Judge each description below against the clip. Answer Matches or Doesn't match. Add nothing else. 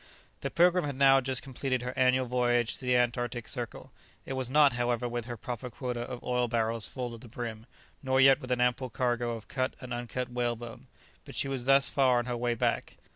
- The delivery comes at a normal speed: Doesn't match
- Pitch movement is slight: Matches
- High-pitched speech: Doesn't match